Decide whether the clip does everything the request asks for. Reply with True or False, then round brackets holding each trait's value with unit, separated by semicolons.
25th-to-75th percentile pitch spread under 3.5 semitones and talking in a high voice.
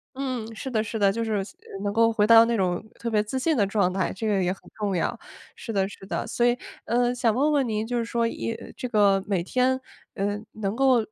True (3.1 semitones; 220 Hz)